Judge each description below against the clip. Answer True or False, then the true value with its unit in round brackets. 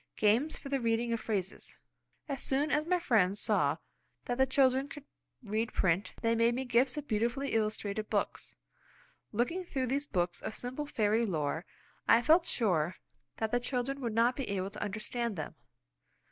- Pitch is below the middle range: False (235 Hz)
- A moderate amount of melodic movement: True (4.1 semitones)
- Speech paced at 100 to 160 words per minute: False (175 wpm)